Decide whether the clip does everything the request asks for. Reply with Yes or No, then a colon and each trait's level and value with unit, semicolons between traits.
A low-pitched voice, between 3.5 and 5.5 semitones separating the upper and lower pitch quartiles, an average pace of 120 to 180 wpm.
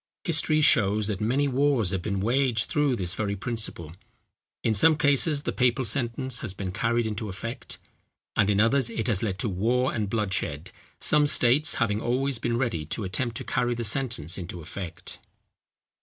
Yes: low, 115 Hz; average, 4.6 semitones; average, 175 wpm